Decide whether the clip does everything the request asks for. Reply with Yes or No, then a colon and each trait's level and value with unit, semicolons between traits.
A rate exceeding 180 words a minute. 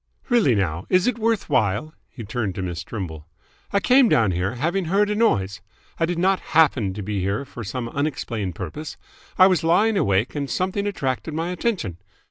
Yes: average, 190 wpm